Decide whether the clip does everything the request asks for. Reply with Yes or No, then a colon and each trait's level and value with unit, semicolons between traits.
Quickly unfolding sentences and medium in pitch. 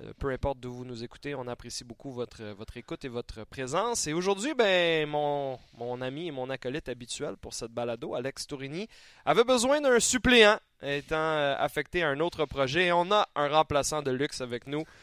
No: average, 195 wpm; medium, 145 Hz